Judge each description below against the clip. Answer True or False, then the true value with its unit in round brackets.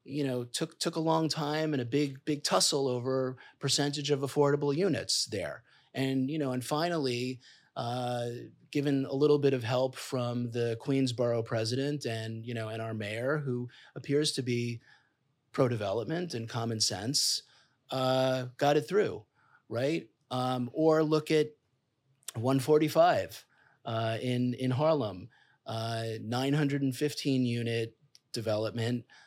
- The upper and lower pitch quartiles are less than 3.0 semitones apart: False (3.3 semitones)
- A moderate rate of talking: True (150 wpm)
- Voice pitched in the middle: False (130 Hz)